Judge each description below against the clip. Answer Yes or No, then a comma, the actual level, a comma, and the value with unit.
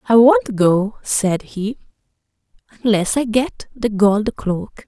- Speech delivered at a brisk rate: No, slow, 135 wpm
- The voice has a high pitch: Yes, high, 215 Hz